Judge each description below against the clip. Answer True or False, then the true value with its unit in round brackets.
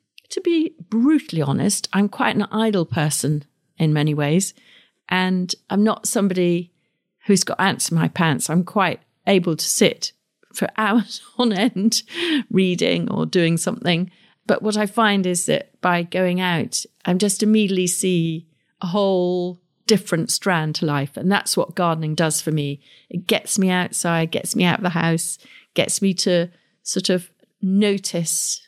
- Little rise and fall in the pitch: False (3.7 semitones)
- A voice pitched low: False (185 Hz)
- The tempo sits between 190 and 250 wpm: False (165 wpm)